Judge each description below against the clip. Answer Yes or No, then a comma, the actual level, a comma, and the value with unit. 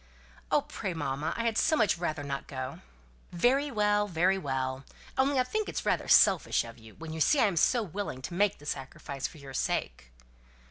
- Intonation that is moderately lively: No, wide, 7.4 semitones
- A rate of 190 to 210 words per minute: Yes, fast, 205 wpm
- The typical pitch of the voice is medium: Yes, medium, 165 Hz